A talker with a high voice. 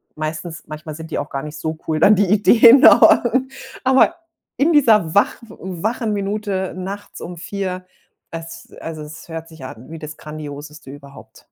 No: medium, 165 Hz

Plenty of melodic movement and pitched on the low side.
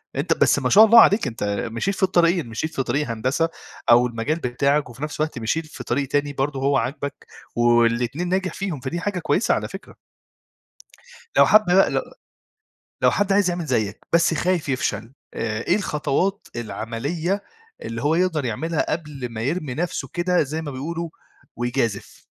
No: wide, 5.9 semitones; medium, 150 Hz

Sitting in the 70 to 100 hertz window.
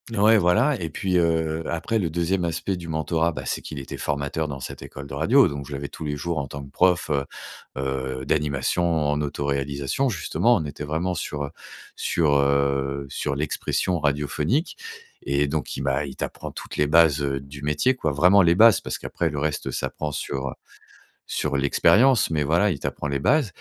Yes: very low, 75 Hz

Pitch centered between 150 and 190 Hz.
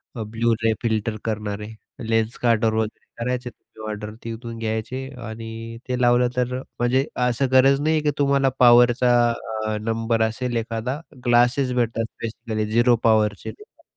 No: low, 115 Hz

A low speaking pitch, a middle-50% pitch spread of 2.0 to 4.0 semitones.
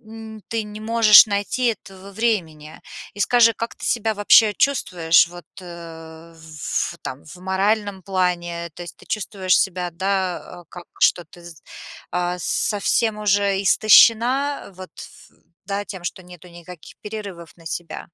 No: high, 190 Hz; average, 3.6 semitones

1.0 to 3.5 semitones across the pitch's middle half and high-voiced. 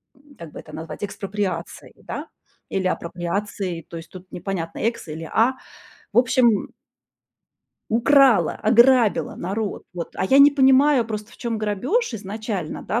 No: average, 5.0 semitones; high, 210 Hz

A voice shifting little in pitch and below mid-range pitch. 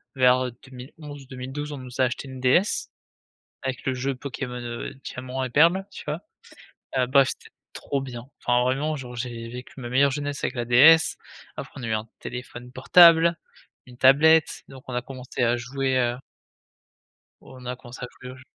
Yes: narrow, 2.2 semitones; low, 130 Hz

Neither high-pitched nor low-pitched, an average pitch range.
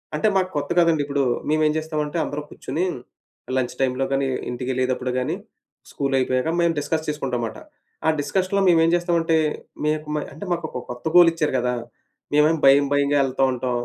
Yes: medium, 145 Hz; average, 3.8 semitones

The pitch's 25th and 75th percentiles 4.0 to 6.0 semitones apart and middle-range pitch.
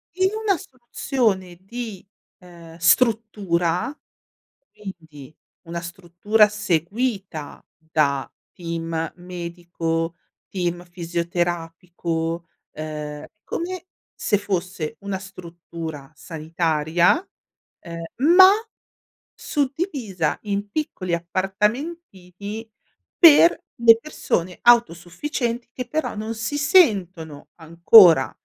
Yes: average, 5.3 semitones; medium, 180 Hz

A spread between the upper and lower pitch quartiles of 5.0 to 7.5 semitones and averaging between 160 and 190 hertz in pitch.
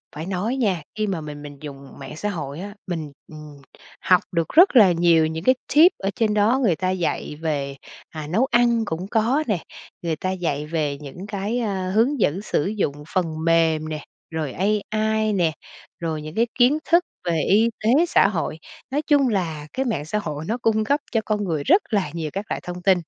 Yes: wide, 5.5 semitones; medium, 185 Hz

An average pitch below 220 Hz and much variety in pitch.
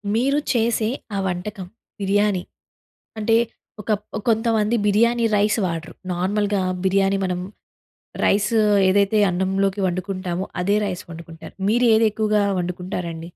No: high, 200 Hz; average, 2.8 semitones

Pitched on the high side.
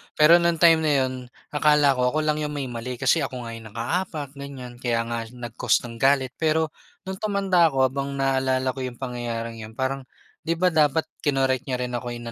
No: low, 135 Hz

